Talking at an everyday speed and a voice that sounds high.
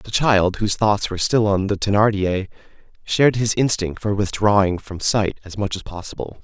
No: average, 185 wpm; low, 100 Hz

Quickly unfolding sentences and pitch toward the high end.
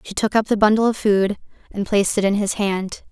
Yes: fast, 250 wpm; high, 205 Hz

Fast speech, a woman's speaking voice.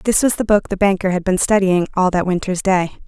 Yes: fast, 255 wpm; female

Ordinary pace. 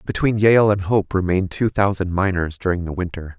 Yes: average, 195 wpm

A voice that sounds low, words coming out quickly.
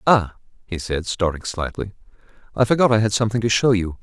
No: low, 105 Hz; average, 195 wpm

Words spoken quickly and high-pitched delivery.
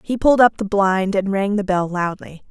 Yes: fast, 240 wpm; high, 200 Hz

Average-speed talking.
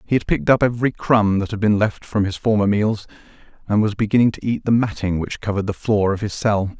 No: fast, 245 wpm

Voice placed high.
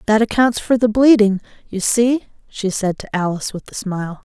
Yes: high, 215 Hz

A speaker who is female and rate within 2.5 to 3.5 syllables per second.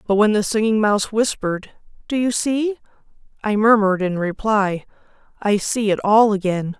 No: female; 5.1 syllables/s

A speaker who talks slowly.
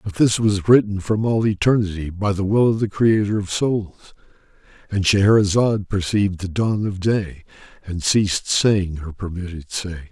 No: average, 160 wpm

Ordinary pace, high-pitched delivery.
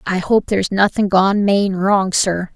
Yes: average, 190 wpm; high, 195 Hz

